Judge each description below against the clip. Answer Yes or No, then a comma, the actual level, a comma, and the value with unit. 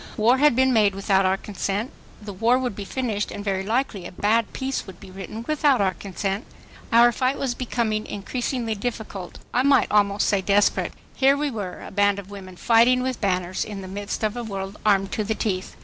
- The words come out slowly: No, fast, 205 wpm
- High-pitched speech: Yes, high, 210 Hz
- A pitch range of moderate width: Yes, average, 3.7 semitones